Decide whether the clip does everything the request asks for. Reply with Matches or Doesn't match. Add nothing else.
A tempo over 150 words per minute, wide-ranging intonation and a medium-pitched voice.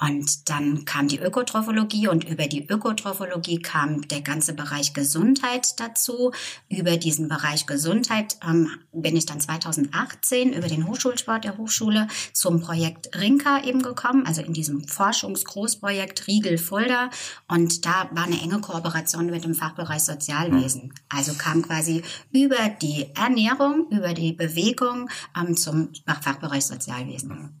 Doesn't match